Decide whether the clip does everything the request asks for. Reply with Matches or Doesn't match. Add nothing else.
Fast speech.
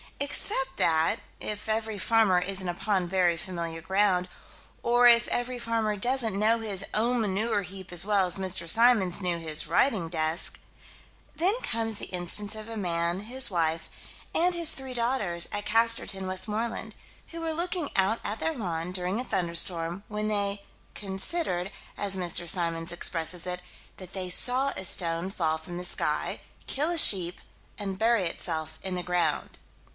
Doesn't match